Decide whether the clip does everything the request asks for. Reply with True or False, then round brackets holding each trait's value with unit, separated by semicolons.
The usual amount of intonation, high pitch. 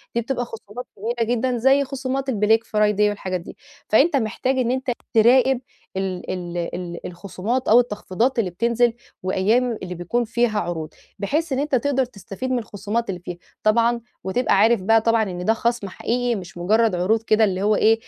True (4.0 semitones; 225 Hz)